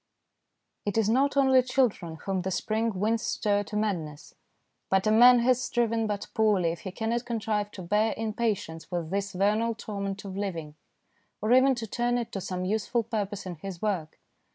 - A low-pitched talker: No, high, 210 Hz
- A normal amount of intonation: Yes, average, 3.2 semitones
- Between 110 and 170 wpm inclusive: No, average, 185 wpm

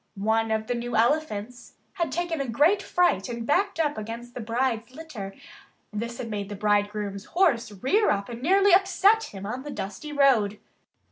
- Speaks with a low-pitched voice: No, high, 240 Hz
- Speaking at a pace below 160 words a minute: No, average, 180 wpm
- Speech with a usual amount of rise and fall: No, wide, 6.8 semitones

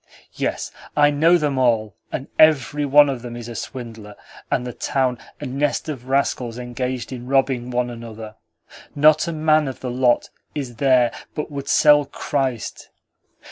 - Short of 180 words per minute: Yes, average, 165 wpm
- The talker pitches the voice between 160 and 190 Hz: No, low, 130 Hz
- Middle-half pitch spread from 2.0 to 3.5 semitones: Yes, average, 3.1 semitones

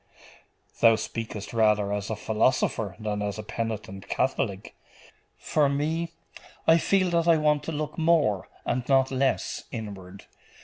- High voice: No, low, 115 Hz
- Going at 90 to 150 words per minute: Yes, average, 140 wpm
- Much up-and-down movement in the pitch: Yes, wide, 6.6 semitones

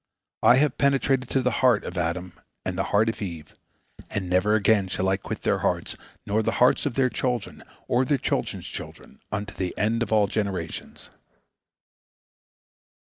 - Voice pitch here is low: Yes, low, 105 Hz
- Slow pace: No, average, 170 wpm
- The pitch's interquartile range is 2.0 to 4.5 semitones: No, average, 4.9 semitones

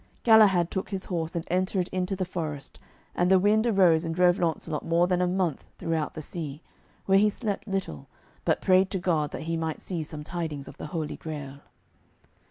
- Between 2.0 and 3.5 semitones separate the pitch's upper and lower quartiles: Yes, average, 3.0 semitones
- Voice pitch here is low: No, medium, 175 Hz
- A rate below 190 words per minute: No, average, 195 wpm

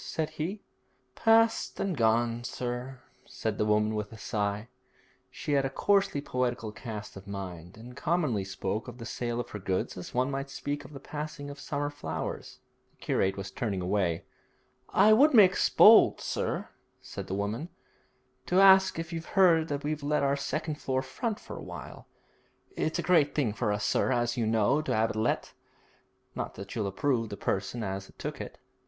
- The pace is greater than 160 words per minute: Yes, average, 190 wpm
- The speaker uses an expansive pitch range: Yes, wide, 6.4 semitones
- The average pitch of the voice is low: Yes, low, 125 Hz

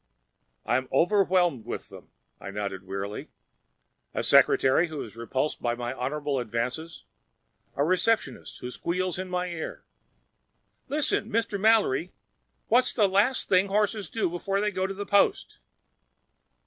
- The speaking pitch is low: No, medium, 175 Hz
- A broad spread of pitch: Yes, wide, 7.9 semitones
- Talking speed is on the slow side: Yes, slow, 130 wpm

